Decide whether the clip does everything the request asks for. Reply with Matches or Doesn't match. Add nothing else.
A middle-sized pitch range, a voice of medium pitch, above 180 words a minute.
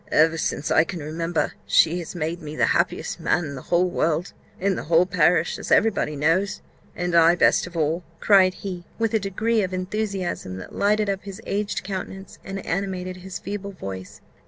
Matches